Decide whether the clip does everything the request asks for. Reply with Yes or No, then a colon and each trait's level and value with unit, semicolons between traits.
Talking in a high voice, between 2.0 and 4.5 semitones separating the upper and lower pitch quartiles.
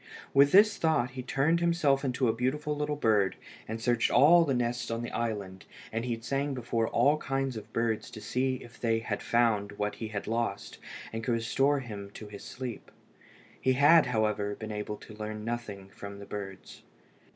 No: low, 115 Hz; average, 4.1 semitones